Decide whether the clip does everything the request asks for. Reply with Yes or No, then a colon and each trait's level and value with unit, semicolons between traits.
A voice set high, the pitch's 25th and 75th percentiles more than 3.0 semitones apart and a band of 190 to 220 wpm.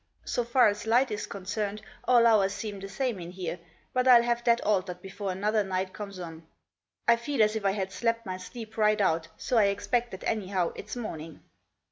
Yes: high, 210 Hz; average, 3.5 semitones; fast, 205 wpm